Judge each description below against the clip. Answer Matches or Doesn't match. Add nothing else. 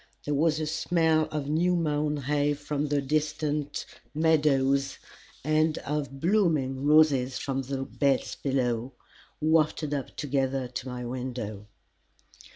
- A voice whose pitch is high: Doesn't match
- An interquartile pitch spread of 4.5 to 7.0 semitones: Doesn't match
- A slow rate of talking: Matches